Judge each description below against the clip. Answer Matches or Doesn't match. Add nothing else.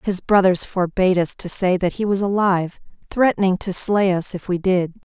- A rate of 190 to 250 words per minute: Matches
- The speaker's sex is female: Matches